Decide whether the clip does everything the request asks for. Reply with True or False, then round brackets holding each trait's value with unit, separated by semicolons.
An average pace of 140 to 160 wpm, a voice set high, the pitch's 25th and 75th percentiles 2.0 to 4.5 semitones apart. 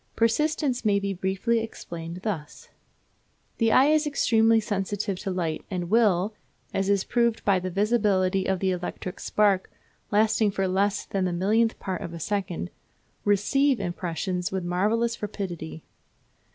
True (145 wpm; 200 Hz; 3.4 semitones)